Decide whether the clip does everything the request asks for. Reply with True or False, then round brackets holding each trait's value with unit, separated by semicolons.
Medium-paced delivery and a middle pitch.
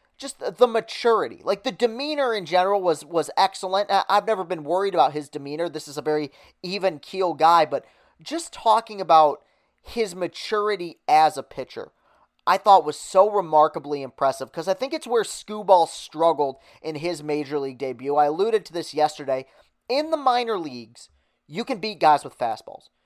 True (175 wpm; 180 Hz)